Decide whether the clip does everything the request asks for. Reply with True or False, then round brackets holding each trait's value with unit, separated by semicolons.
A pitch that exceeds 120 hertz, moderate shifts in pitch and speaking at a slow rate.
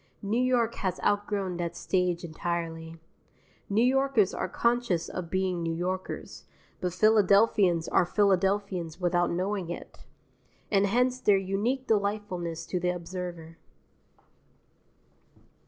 True (185 Hz; 3.1 semitones; 115 wpm)